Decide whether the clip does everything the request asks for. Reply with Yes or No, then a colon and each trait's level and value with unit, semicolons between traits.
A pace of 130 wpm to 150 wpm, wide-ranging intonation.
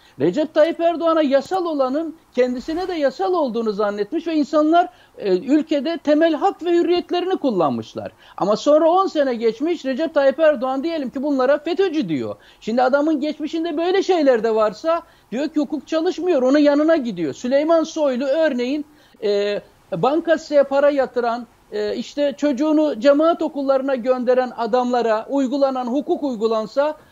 No: fast, 140 wpm; average, 3.9 semitones